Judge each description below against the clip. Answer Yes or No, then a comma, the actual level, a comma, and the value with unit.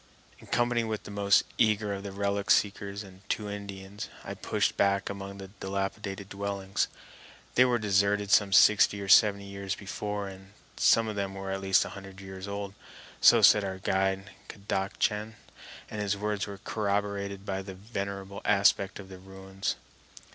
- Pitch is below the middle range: Yes, low, 100 Hz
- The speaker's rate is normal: Yes, average, 170 wpm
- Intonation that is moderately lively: No, narrow, 1.0 semitones